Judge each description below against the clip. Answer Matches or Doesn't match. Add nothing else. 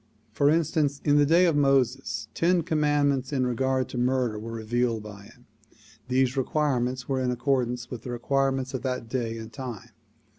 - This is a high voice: Doesn't match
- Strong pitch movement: Doesn't match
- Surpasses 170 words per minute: Matches